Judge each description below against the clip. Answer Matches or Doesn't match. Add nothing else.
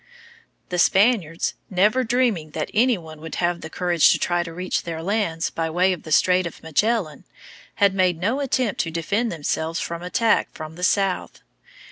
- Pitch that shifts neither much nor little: Matches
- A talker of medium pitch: Matches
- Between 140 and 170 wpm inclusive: Doesn't match